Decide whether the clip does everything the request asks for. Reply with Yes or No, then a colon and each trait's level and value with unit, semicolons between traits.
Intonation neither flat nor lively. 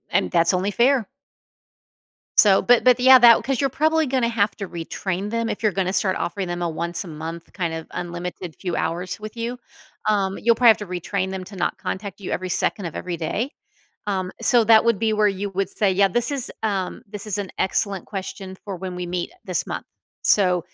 Yes: average, 3.8 semitones